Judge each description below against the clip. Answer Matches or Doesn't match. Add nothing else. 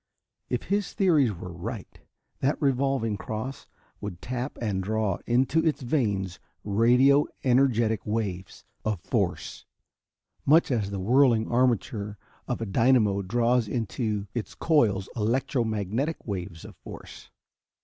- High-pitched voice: Doesn't match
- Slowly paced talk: Matches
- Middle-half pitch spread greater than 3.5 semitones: Matches